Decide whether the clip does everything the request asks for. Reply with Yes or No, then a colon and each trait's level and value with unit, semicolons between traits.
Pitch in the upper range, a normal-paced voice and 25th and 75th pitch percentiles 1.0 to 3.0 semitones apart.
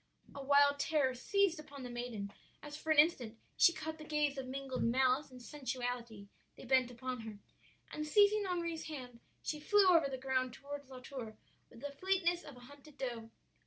No: very high, 275 Hz; average, 190 wpm; average, 3.5 semitones